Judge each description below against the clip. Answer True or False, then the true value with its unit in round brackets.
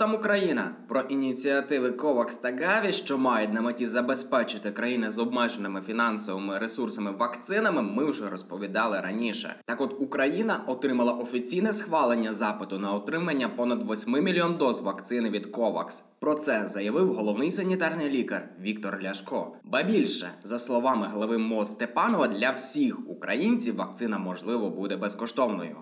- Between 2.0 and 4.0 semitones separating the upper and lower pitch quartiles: False (4.8 semitones)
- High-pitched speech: False (120 Hz)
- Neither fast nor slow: True (140 wpm)